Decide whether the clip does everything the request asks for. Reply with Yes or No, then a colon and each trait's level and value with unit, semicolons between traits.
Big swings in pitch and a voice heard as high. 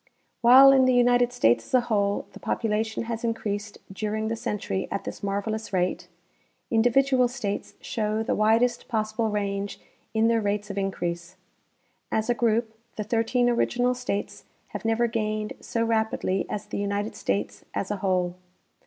No: average, 2.8 semitones; high, 220 Hz